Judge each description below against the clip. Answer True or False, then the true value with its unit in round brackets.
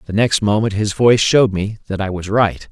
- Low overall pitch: True (105 Hz)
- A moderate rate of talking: False (245 wpm)